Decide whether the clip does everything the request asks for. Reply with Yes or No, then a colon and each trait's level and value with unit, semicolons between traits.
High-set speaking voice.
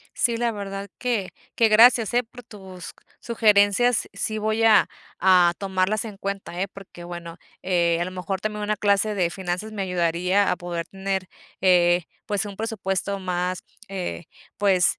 Yes: high, 195 Hz